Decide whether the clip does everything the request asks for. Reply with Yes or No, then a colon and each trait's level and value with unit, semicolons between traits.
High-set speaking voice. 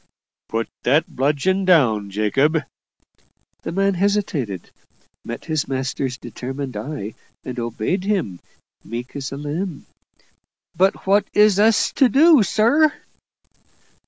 No: medium, 150 Hz